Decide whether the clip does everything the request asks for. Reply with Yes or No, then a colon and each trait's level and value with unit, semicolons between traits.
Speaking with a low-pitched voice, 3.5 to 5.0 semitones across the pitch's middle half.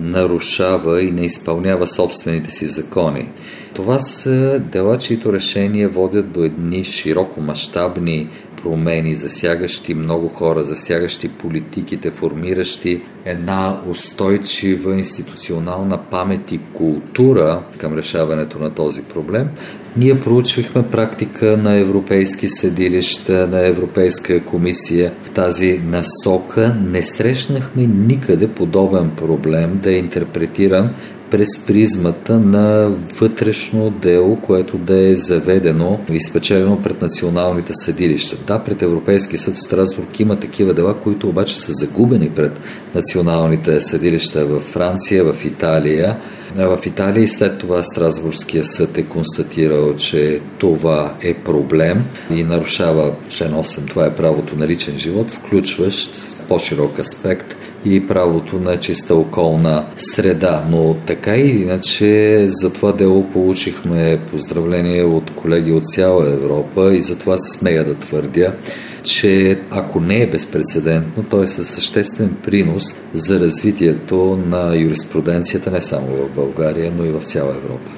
No: very low, 90 Hz; average, 3.1 semitones